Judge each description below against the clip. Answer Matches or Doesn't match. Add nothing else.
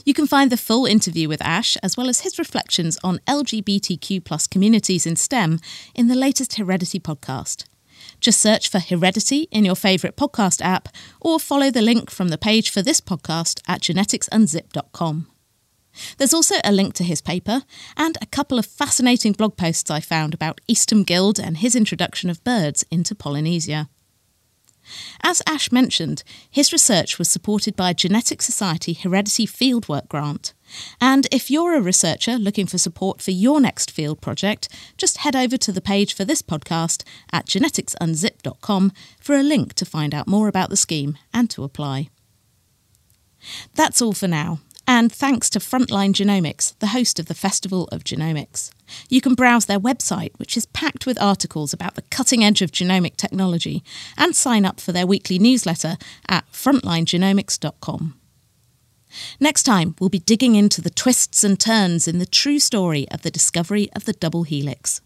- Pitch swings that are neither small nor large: Doesn't match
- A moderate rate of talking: Matches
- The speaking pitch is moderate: Doesn't match